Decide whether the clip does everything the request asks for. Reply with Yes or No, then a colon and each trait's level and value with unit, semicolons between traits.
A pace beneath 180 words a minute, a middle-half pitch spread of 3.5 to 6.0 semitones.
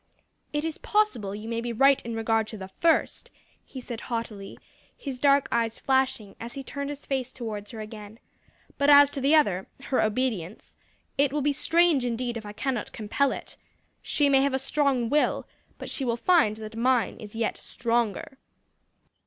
No: average, 185 wpm; average, 4.0 semitones